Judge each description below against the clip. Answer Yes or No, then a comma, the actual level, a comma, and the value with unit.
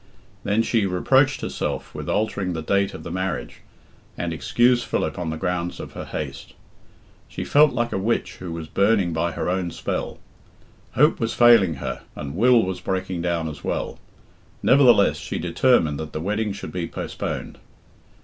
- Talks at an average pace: Yes, average, 170 wpm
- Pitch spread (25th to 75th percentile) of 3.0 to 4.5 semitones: No, average, 5.3 semitones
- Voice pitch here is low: Yes, very low, 95 Hz